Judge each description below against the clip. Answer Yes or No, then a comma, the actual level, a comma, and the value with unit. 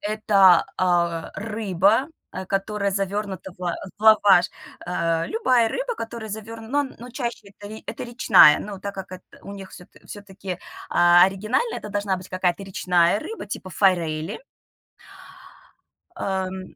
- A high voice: Yes, high, 195 Hz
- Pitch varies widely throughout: No, average, 2.9 semitones